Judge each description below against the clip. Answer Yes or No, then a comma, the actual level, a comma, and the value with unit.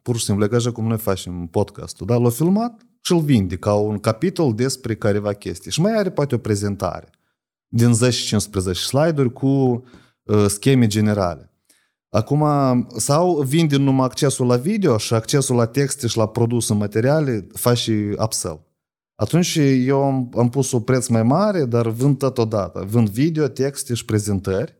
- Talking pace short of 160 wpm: No, fast, 170 wpm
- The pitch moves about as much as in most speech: Yes, average, 4.6 semitones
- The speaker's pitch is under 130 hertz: Yes, low, 120 Hz